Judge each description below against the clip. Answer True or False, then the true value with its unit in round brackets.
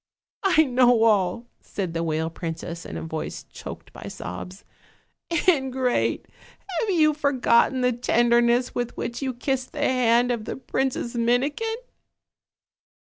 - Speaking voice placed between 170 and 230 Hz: False (245 Hz)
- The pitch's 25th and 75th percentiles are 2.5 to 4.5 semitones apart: True (3.3 semitones)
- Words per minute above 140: False (135 wpm)